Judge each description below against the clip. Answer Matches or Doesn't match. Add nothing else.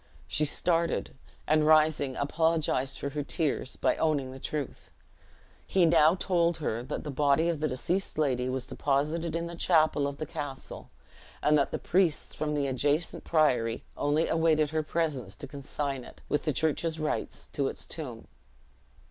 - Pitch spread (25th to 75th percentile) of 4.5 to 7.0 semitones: Doesn't match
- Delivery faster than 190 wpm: Doesn't match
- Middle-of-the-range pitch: Matches